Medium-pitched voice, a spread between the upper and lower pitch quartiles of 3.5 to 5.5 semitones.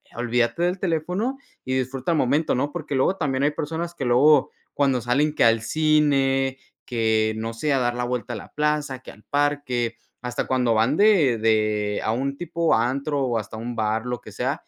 No: low, 130 Hz; average, 4.2 semitones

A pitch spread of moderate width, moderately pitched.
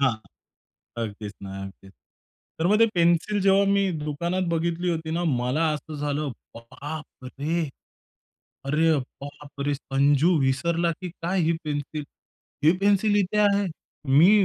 Yes: average, 4.1 semitones; medium, 160 Hz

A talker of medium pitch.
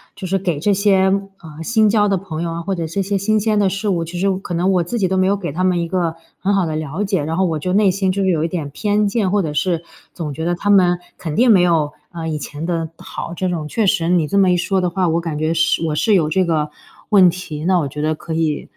Yes: medium, 180 Hz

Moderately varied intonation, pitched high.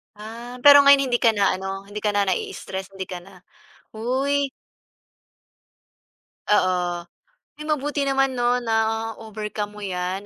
Yes: average, 4.7 semitones; high, 220 Hz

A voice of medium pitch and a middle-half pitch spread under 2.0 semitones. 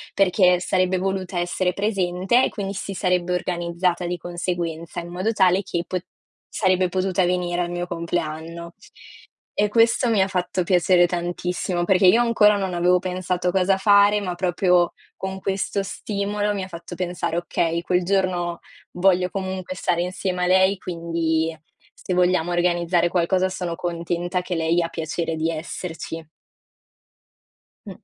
Yes: medium, 180 Hz; narrow, 1.6 semitones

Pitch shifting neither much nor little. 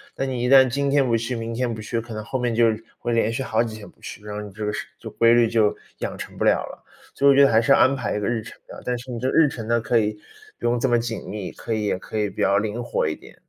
No: narrow, 2.3 semitones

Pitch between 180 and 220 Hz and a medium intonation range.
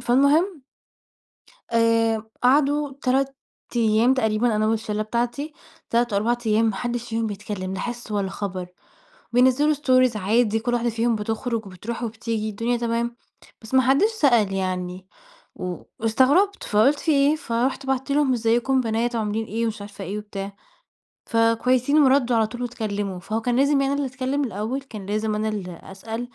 No: high, 230 Hz; average, 3.2 semitones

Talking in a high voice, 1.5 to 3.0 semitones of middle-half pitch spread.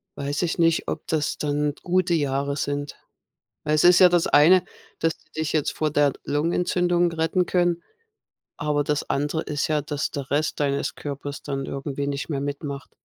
No: medium, 150 Hz; narrow, 2.6 semitones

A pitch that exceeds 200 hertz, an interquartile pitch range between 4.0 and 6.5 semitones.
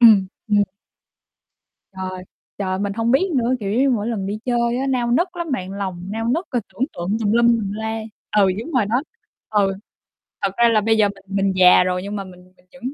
No: high, 215 Hz; average, 3.4 semitones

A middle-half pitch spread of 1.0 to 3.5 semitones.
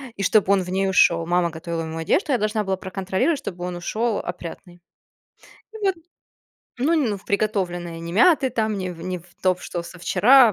No: average, 4.1 semitones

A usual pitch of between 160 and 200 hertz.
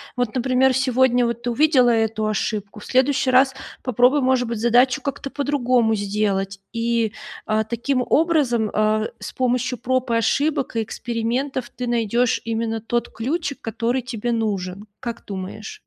No: high, 240 Hz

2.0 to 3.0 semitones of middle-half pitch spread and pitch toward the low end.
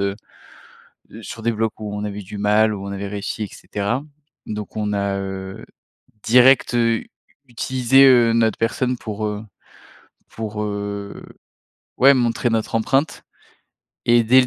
Yes: average, 2.7 semitones; low, 110 Hz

